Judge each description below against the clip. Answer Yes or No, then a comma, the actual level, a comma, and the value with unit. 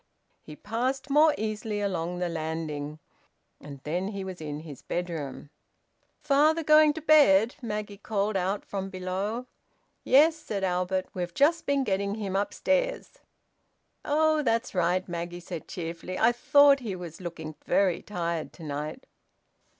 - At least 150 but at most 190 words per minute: No, average, 140 wpm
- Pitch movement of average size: No, wide, 6.7 semitones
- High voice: Yes, high, 195 Hz